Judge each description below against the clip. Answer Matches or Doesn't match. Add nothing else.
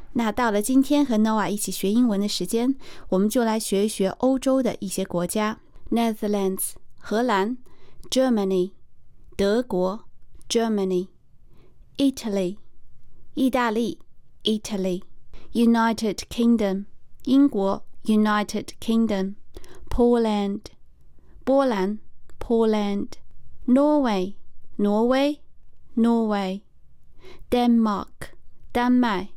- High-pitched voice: Matches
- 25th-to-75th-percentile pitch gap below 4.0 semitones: Matches